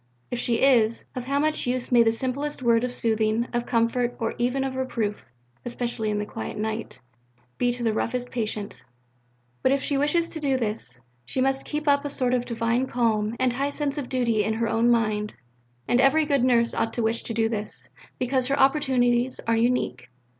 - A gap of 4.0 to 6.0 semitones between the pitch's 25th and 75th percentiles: No, narrow, 2.6 semitones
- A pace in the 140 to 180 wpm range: No, fast, 205 wpm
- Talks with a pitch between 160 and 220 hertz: No, high, 245 Hz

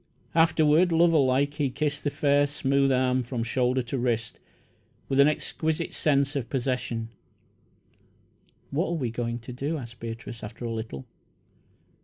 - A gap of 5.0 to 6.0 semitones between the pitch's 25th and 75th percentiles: No, average, 3.6 semitones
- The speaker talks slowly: No, average, 150 wpm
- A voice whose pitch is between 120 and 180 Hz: Yes, low, 135 Hz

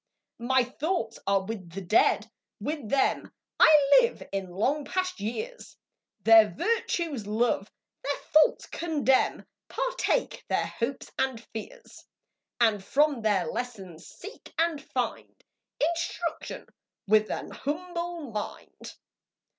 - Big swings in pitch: Yes, wide, 7.6 semitones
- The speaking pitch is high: Yes, very high, 265 Hz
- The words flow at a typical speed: No, slow, 115 wpm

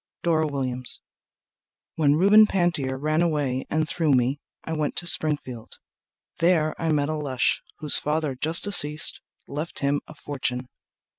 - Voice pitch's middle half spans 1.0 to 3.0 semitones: Yes, average, 2.7 semitones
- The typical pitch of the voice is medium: Yes, medium, 150 Hz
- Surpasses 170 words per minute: No, average, 145 wpm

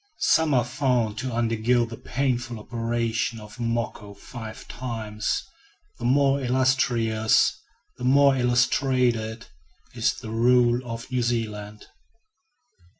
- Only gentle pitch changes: Yes, narrow, 2.2 semitones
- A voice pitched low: Yes, low, 120 Hz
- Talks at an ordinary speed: No, slow, 110 wpm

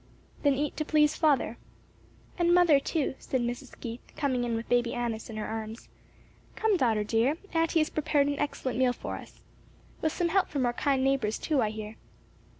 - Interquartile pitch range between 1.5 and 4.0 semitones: No, average, 4.6 semitones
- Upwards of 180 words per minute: Yes, average, 190 wpm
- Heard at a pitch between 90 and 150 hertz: No, very high, 265 Hz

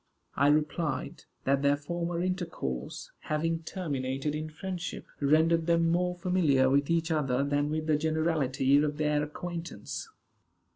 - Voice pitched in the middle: Yes, medium, 155 Hz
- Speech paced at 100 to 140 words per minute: Yes, slow, 135 wpm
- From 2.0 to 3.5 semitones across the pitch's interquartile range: Yes, average, 2.9 semitones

